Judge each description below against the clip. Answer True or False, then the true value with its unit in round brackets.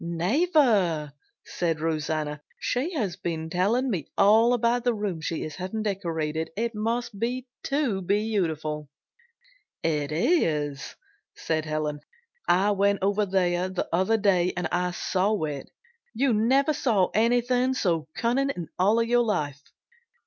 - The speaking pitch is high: True (195 Hz)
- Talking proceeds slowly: True (130 wpm)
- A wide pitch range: True (6.4 semitones)